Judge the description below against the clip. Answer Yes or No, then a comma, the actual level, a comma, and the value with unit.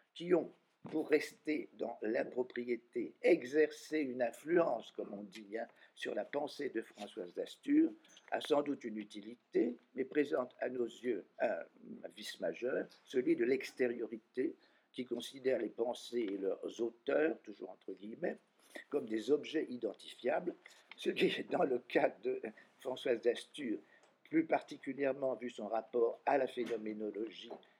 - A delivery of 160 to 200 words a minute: No, slow, 145 wpm